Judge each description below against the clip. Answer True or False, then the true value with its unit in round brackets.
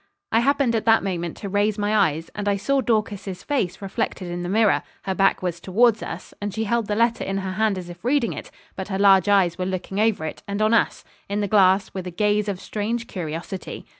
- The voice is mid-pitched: False (200 Hz)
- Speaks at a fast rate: True (235 wpm)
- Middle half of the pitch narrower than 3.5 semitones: True (2.7 semitones)